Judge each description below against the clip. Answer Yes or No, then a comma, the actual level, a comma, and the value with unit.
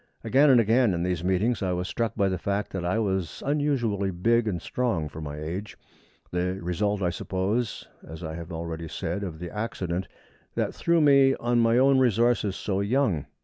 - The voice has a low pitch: Yes, low, 100 Hz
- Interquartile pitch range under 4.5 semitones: No, average, 5.0 semitones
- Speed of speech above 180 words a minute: Yes, average, 190 wpm